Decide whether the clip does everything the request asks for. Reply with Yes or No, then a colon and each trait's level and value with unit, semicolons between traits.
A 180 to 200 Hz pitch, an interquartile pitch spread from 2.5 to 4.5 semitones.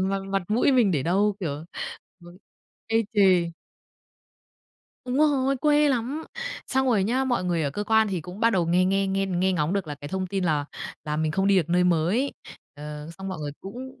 No: high, 190 Hz; average, 4.9 semitones